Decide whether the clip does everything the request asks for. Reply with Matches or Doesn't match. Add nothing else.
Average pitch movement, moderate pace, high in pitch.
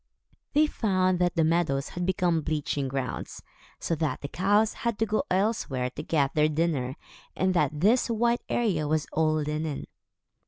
Doesn't match